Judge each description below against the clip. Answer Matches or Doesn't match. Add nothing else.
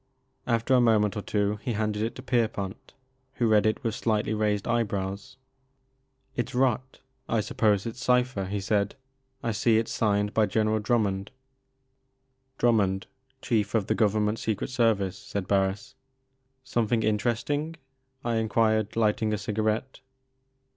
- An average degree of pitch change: Matches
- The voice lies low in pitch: Matches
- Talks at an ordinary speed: Matches